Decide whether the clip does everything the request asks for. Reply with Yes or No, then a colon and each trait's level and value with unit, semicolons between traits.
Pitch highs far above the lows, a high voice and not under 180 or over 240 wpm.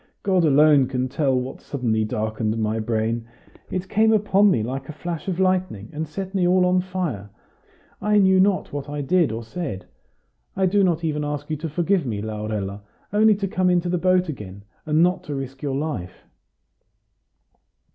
No: wide, 7.9 semitones; medium, 155 Hz; average, 185 wpm